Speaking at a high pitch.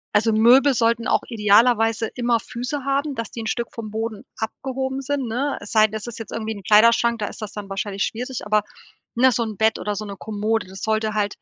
Yes: high, 225 Hz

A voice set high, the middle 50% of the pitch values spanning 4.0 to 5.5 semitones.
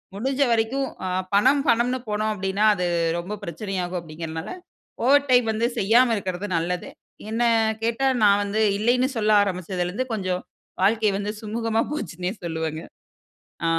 Yes: high, 210 Hz; average, 4.4 semitones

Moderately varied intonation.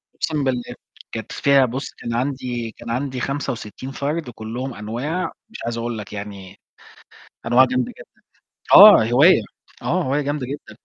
Yes: average, 3.2 semitones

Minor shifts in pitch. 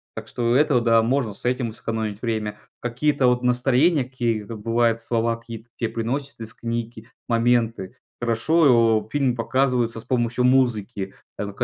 Yes: narrow, 1.8 semitones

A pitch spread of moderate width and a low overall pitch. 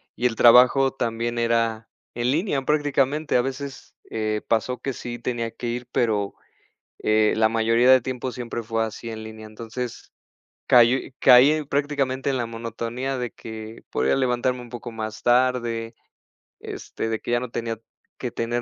No: narrow, 2.1 semitones; low, 120 Hz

